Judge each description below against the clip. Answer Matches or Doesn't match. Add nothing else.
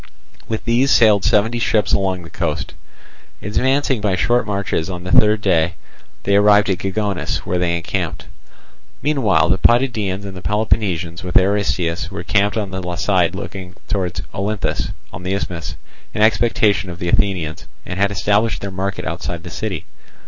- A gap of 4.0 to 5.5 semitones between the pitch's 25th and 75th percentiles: Doesn't match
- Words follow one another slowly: Doesn't match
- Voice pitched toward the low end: Matches